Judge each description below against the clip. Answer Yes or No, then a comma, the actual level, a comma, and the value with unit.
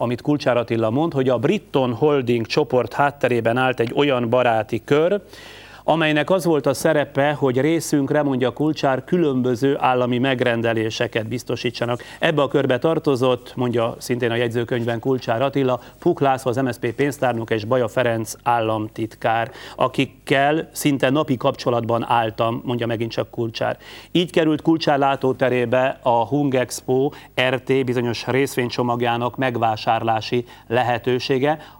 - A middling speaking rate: Yes, average, 130 wpm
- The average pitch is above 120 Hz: Yes, low, 130 Hz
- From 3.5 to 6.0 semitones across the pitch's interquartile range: No, average, 2.9 semitones